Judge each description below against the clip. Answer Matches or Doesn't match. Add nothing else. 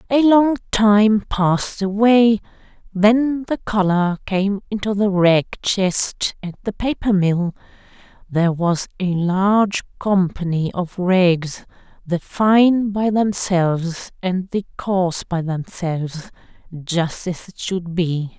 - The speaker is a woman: Matches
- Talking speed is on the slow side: Matches